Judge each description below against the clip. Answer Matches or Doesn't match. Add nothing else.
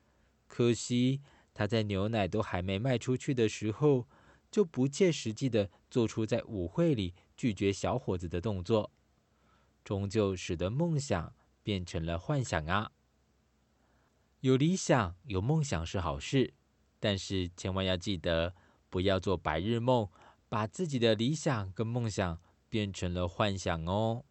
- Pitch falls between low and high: Doesn't match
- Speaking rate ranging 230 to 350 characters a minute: Doesn't match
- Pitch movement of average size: Matches